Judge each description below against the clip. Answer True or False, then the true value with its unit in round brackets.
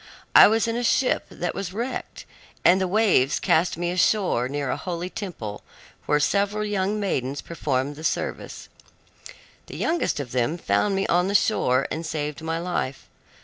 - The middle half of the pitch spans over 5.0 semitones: True (5.6 semitones)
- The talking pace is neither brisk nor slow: True (170 wpm)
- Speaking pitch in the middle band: True (175 Hz)